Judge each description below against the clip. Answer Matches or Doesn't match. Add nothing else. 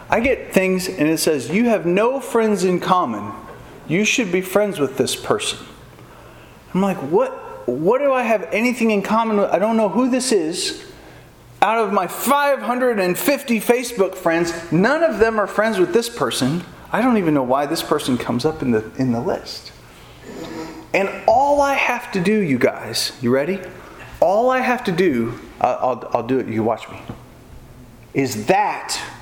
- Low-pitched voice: Doesn't match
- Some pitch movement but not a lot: Doesn't match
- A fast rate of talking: Doesn't match